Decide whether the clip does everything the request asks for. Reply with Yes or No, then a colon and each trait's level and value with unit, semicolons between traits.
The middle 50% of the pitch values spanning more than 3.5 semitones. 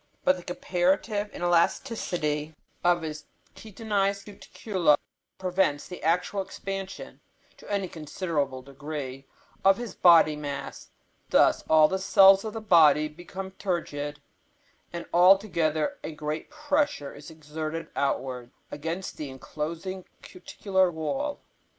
Yes: average, 4.2 semitones